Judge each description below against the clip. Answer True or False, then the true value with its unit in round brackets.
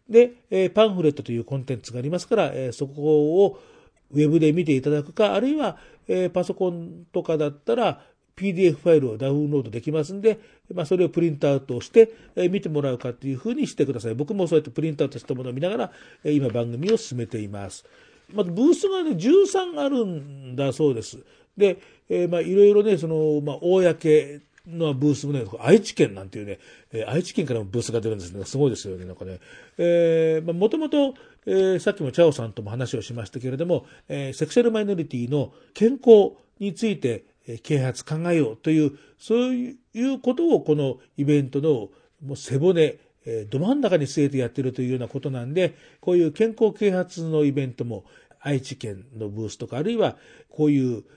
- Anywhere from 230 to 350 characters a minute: False (375 characters per minute)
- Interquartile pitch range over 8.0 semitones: False (6.3 semitones)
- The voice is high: False (150 Hz)